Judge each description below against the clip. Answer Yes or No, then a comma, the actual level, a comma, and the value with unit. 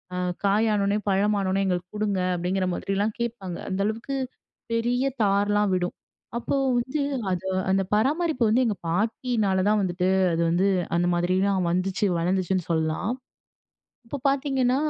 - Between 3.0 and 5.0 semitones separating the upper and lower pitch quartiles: Yes, average, 3.8 semitones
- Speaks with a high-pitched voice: Yes, high, 200 Hz